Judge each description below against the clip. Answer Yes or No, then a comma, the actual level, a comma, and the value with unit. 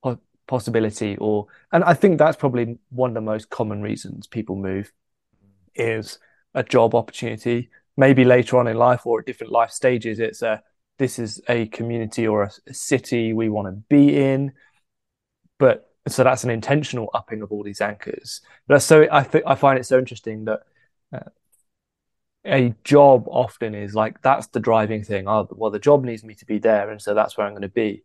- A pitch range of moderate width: Yes, average, 3.2 semitones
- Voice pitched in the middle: No, low, 115 Hz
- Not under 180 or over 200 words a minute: Yes, average, 195 wpm